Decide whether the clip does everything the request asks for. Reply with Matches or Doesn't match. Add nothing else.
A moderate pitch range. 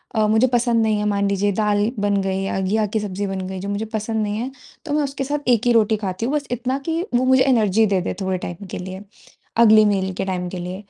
Matches